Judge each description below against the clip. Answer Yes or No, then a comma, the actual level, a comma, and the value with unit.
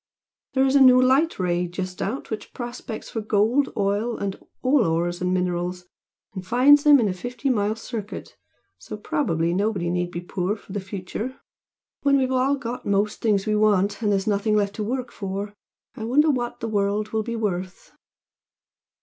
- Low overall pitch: No, high, 210 Hz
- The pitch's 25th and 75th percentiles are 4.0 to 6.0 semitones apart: Yes, average, 4.6 semitones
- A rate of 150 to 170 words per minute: No, average, 185 wpm